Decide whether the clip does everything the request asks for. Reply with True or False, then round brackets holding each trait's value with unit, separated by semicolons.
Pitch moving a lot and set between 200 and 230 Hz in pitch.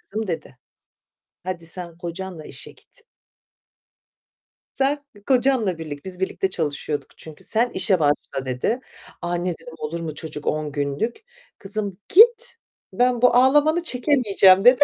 False (7.6 semitones; 190 Hz)